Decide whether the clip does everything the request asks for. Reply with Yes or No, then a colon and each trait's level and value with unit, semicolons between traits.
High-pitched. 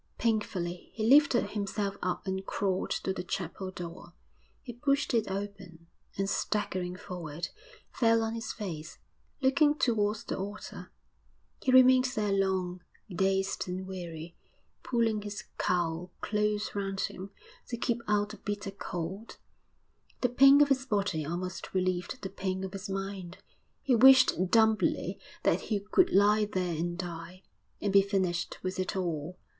Yes: high, 195 Hz